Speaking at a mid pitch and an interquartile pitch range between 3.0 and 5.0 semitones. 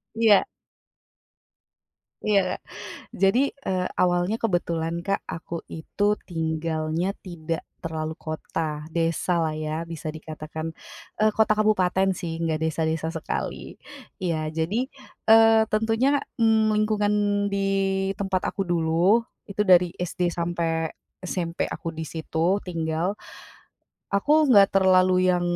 Yes: medium, 175 Hz; average, 3.7 semitones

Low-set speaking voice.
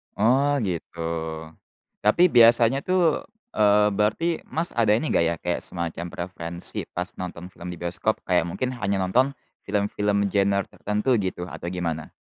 Yes: low, 100 Hz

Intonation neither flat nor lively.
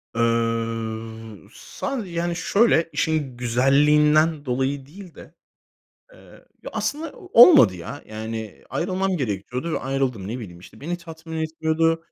No: wide, 6.3 semitones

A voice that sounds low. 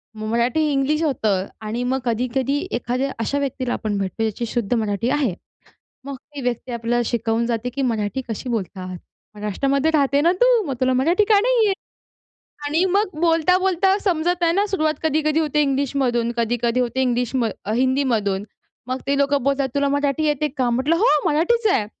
No: very high, 265 Hz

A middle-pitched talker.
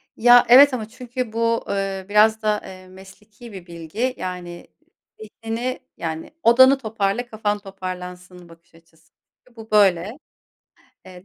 No: high, 210 Hz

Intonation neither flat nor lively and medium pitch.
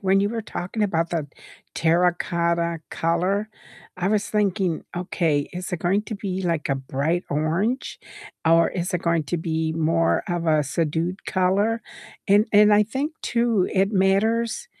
Yes: average, 3.7 semitones; medium, 180 Hz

